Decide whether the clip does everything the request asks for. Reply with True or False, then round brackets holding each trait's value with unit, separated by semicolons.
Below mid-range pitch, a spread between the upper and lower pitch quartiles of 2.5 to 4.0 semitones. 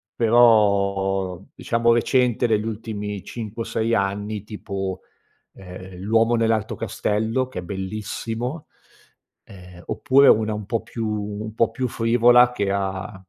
True (110 Hz; 2.8 semitones)